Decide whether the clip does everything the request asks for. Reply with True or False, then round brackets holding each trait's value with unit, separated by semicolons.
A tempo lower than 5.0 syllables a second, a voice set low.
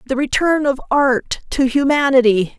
False (4.5 syllables/s; 265 Hz)